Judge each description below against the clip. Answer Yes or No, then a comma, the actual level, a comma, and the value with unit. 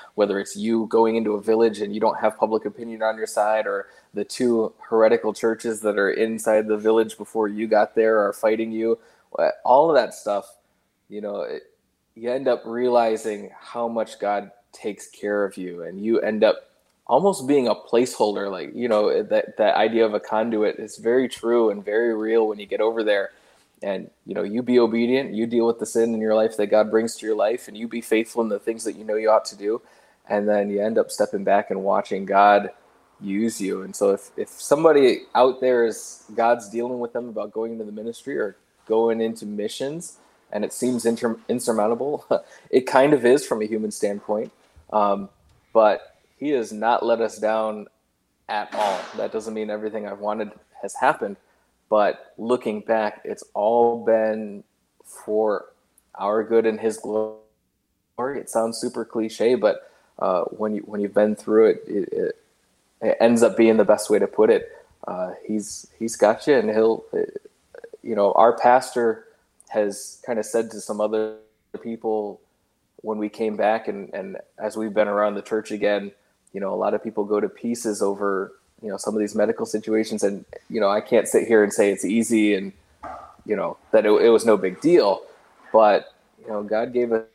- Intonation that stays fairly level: Yes, narrow, 1.8 semitones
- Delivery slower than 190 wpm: No, average, 200 wpm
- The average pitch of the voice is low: Yes, low, 110 Hz